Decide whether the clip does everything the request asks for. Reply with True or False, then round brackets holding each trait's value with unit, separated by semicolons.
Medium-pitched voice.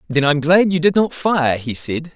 True (155 Hz)